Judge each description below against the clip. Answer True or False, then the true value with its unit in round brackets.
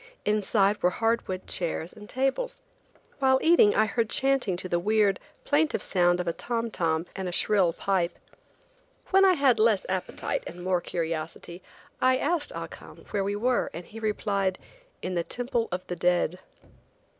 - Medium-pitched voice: False (200 Hz)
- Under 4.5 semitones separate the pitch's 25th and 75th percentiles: False (5.1 semitones)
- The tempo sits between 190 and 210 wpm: False (170 wpm)